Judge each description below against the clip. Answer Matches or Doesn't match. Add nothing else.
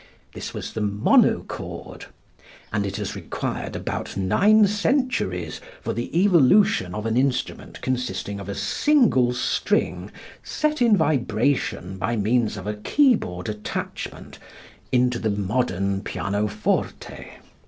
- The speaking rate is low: Matches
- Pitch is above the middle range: Doesn't match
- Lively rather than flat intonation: Matches